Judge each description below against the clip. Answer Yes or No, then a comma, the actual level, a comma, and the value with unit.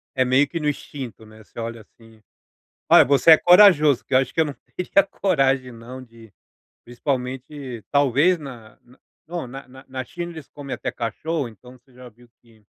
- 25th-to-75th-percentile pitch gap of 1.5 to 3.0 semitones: No, average, 3.6 semitones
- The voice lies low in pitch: Yes, low, 130 Hz